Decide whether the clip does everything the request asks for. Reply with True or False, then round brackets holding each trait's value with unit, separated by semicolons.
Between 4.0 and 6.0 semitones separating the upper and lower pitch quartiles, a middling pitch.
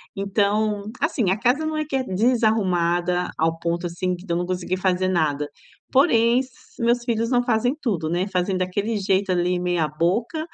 False (4.6 semitones; 195 Hz)